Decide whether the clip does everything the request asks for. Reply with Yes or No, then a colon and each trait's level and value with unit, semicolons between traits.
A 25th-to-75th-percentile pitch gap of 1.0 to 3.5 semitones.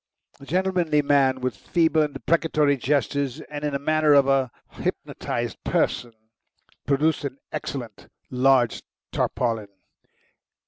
Yes: average, 2.7 semitones